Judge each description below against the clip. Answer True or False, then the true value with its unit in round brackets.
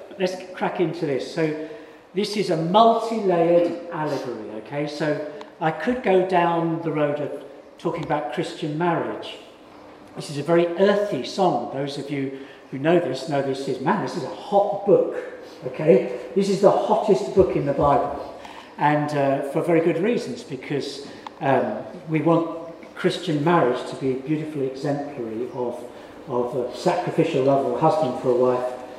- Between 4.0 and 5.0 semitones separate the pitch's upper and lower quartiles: True (4.3 semitones)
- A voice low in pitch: False (160 Hz)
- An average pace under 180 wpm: True (170 wpm)